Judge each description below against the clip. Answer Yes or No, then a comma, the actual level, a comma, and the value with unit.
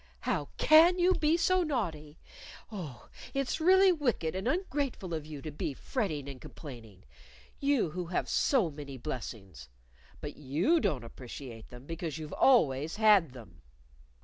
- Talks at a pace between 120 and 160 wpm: Yes, average, 150 wpm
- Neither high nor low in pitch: Yes, medium, 160 Hz